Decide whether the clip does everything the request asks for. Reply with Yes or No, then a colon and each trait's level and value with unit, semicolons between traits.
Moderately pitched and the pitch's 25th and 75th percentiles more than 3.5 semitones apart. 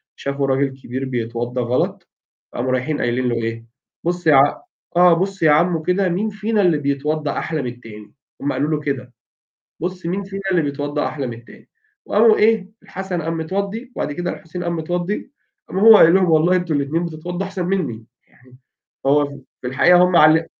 Yes: medium, 160 Hz; average, 5.0 semitones